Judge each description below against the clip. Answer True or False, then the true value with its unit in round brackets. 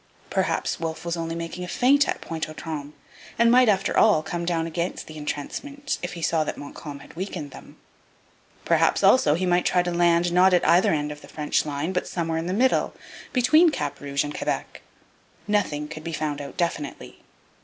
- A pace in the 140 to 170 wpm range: False (200 wpm)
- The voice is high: False (170 Hz)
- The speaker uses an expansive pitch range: False (3.2 semitones)